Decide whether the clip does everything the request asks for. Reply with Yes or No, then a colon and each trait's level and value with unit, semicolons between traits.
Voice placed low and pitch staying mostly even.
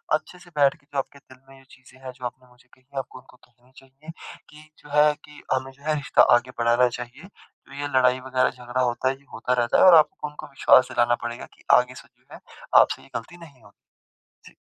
Yes: low, 130 Hz; narrow, 2.3 semitones